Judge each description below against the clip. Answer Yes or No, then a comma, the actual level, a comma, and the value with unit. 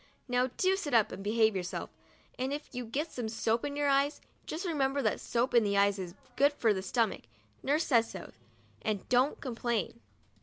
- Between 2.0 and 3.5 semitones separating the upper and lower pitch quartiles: No, average, 4.5 semitones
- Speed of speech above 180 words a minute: Yes, average, 200 wpm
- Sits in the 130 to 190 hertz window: No, high, 245 Hz